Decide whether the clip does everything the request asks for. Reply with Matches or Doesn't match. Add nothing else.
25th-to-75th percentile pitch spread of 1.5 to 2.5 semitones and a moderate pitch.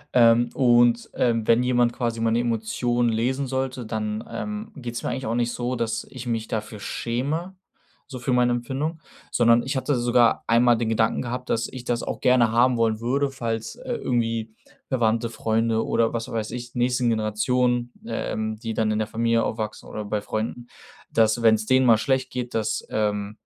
Doesn't match